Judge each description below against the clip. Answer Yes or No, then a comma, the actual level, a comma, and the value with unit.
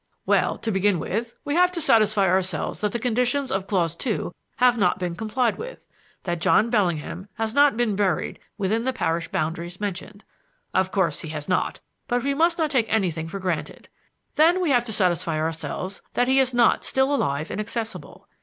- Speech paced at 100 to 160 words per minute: No, average, 190 wpm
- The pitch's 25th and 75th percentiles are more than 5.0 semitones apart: Yes, wide, 5.5 semitones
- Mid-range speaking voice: No, high, 210 Hz